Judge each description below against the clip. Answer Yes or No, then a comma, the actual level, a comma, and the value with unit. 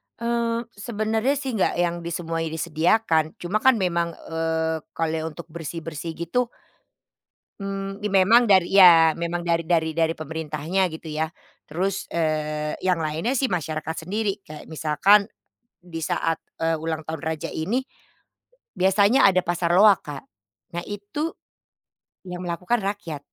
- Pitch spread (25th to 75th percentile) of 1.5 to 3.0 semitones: No, average, 3.6 semitones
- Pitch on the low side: No, medium, 170 Hz